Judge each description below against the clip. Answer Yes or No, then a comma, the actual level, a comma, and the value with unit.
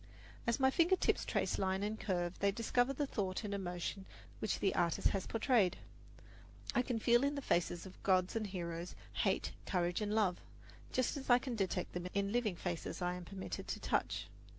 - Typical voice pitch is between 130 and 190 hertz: No, high, 200 Hz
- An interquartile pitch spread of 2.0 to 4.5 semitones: No, average, 4.9 semitones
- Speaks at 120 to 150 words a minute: No, average, 195 wpm